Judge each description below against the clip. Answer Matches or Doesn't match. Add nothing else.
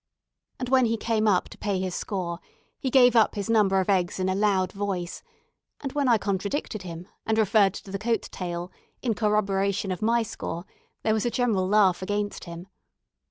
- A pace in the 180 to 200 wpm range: Matches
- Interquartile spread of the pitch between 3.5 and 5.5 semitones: Doesn't match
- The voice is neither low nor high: Doesn't match